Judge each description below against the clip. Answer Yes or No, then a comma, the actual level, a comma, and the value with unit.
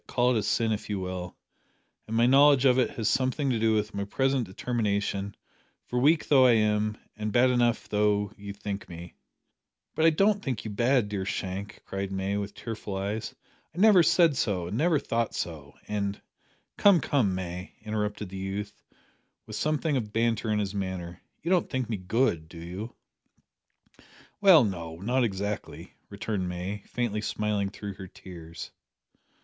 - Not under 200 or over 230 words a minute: No, average, 175 wpm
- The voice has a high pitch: No, low, 105 Hz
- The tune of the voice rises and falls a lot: No, average, 4.2 semitones